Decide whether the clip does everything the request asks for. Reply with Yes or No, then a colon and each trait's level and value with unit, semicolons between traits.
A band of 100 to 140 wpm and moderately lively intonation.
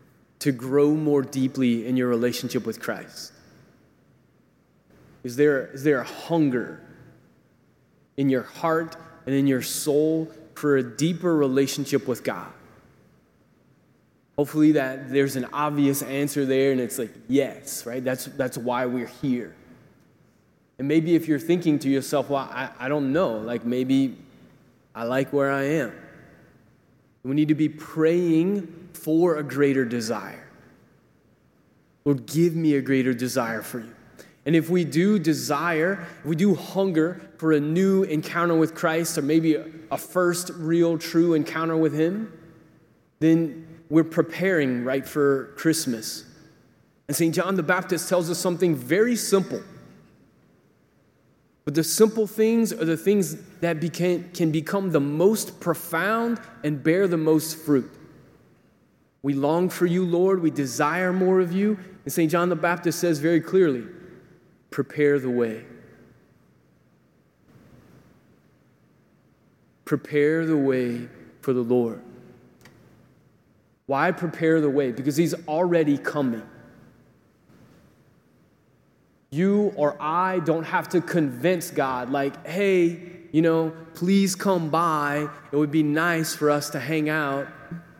Yes: slow, 135 wpm; average, 3.8 semitones